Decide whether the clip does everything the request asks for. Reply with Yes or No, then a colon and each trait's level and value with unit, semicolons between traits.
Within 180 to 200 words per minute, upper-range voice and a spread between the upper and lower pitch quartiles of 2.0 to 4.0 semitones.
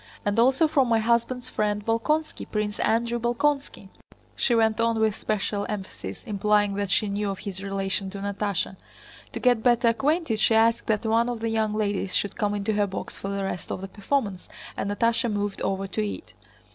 Yes: average, 195 wpm; high, 215 Hz; narrow, 2.6 semitones